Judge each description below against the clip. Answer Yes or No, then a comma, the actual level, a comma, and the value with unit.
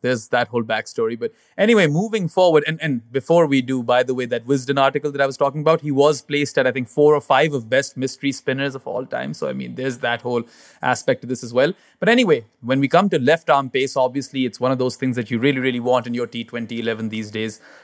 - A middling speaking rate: No, fast, 255 wpm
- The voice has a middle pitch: No, low, 130 Hz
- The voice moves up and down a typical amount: Yes, average, 3.0 semitones